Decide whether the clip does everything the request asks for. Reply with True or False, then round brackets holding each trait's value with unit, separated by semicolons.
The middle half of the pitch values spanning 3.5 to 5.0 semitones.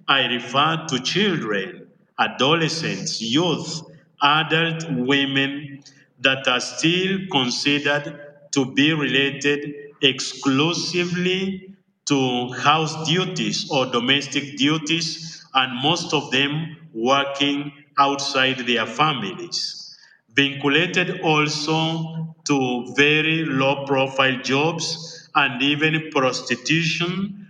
False (3.0 semitones)